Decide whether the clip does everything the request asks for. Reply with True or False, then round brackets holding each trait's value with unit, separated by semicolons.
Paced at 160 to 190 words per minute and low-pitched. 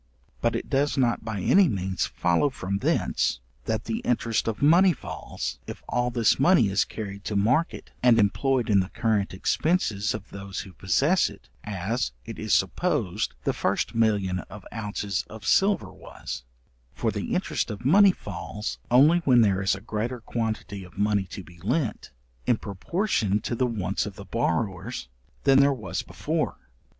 True (170 wpm; 110 Hz)